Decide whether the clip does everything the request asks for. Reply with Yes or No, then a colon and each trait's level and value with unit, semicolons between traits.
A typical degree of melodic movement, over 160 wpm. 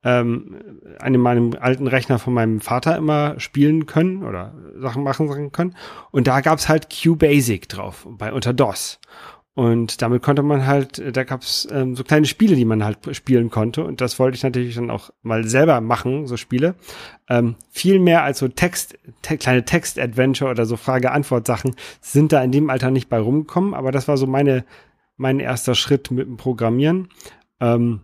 Yes: average, 3.3 semitones; average, 180 wpm